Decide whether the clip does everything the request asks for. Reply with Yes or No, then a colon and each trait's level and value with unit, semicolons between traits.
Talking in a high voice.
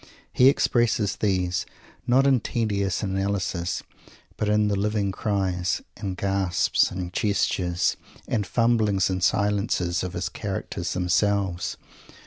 No: low, 100 Hz